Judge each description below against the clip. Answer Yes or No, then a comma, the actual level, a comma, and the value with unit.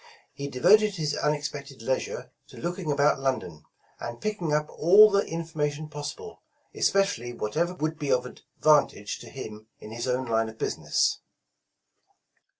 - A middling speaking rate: Yes, average, 150 wpm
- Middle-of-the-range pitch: Yes, medium, 150 Hz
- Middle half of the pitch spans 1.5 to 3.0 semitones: No, average, 5.1 semitones